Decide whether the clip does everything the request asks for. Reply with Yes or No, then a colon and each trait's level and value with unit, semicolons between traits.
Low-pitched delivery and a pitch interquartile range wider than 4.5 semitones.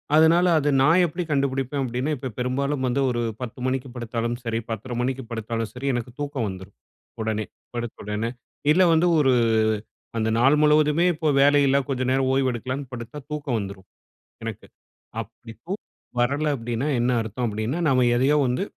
No: low, 130 Hz; average, 3.6 semitones